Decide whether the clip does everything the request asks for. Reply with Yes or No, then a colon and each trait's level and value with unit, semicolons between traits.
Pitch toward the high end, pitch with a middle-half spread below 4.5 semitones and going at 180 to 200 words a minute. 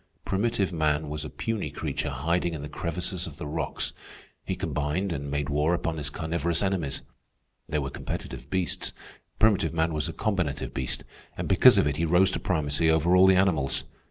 No: very low, 80 Hz; average, 3.7 semitones; average, 185 wpm